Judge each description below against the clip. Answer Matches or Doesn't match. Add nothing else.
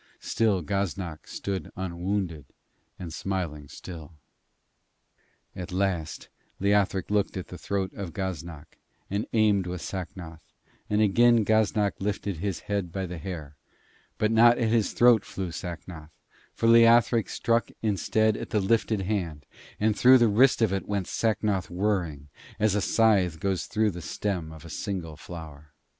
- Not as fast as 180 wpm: Matches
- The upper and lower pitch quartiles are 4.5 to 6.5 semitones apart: Doesn't match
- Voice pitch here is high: Doesn't match